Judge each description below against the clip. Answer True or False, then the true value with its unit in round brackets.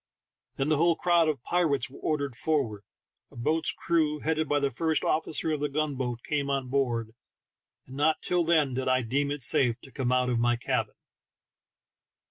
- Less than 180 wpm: False (190 wpm)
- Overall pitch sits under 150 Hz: True (140 Hz)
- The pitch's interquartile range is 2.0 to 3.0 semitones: False (3.6 semitones)